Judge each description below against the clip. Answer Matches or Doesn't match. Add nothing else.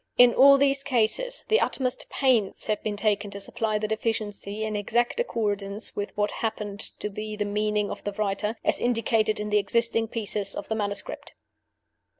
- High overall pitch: Matches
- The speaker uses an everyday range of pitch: Doesn't match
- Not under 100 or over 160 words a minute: Doesn't match